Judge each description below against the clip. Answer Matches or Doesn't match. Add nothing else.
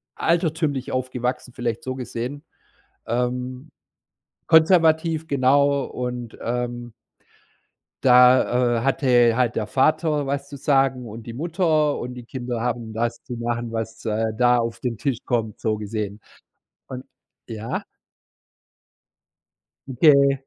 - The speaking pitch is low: Matches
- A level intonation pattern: Doesn't match